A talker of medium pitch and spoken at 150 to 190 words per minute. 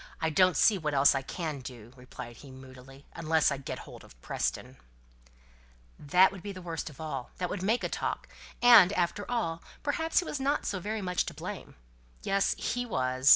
No: medium, 165 Hz; average, 200 wpm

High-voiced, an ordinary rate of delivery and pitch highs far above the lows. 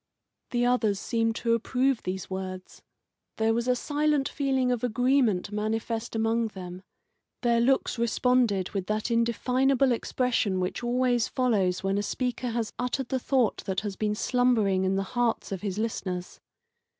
No: high, 230 Hz; average, 155 wpm; average, 3.8 semitones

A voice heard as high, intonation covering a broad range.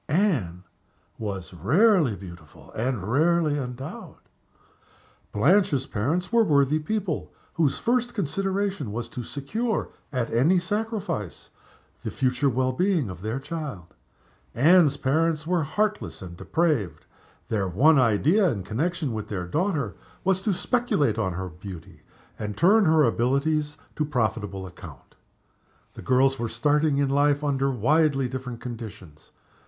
No: medium, 140 Hz; wide, 7.3 semitones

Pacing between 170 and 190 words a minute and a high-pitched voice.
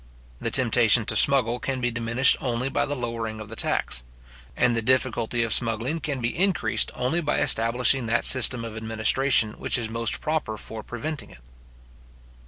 No: average, 175 wpm; low, 120 Hz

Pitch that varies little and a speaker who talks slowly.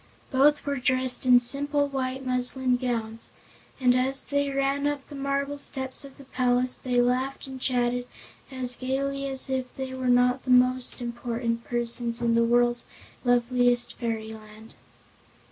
No: narrow, 1.8 semitones; average, 150 wpm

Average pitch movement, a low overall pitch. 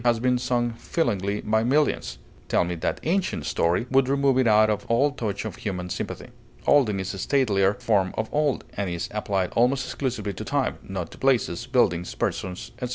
Yes: average, 5.0 semitones; low, 110 Hz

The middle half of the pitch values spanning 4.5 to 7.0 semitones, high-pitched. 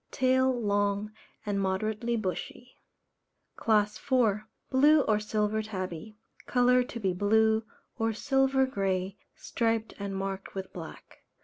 No: average, 3.6 semitones; high, 215 Hz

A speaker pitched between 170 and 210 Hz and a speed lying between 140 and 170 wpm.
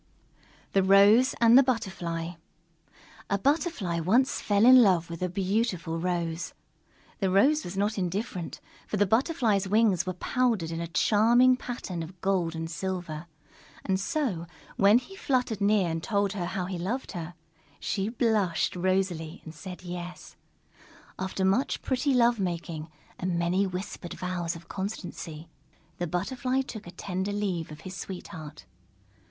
Yes: high, 190 Hz; average, 150 wpm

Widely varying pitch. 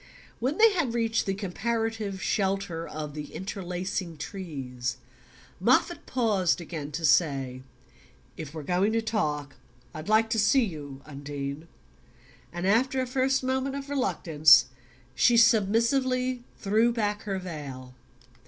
Yes: wide, 7.1 semitones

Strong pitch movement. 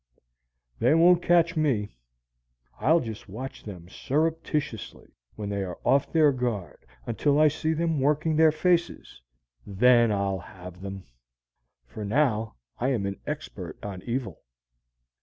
Yes: wide, 7.6 semitones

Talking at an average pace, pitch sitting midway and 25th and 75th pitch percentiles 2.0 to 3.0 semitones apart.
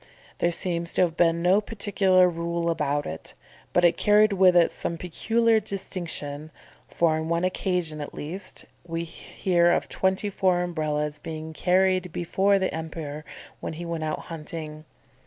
Yes: average, 155 wpm; medium, 170 Hz; average, 2.7 semitones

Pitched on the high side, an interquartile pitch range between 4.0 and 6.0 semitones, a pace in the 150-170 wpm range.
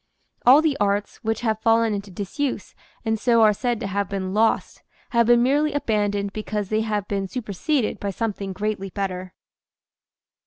No: high, 215 Hz; average, 2.7 semitones; average, 165 wpm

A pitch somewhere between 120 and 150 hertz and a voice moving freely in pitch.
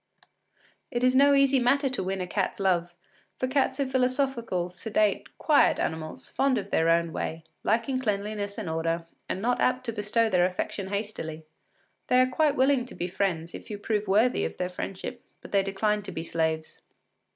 No: high, 205 Hz; wide, 5.9 semitones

